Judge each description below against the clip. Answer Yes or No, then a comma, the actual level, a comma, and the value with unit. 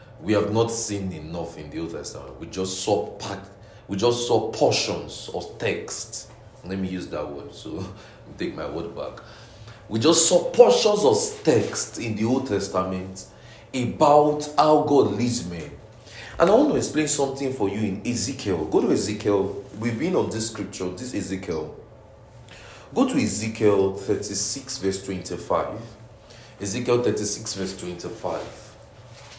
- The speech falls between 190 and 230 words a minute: No, average, 155 wpm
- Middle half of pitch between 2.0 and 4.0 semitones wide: Yes, average, 3.7 semitones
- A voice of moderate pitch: No, low, 110 Hz